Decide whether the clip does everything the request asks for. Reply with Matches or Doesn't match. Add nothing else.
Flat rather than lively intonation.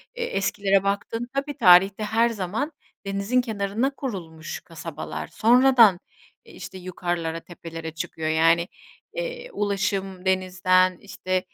Doesn't match